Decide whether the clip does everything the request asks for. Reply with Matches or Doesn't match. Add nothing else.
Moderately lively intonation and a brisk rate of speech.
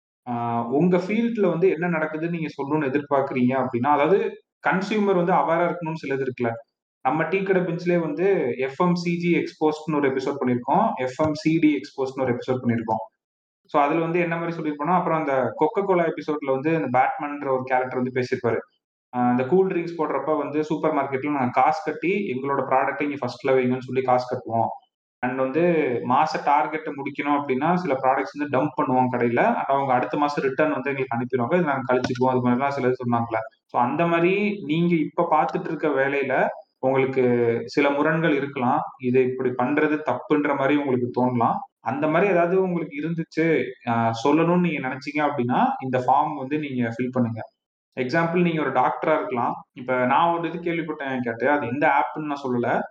Matches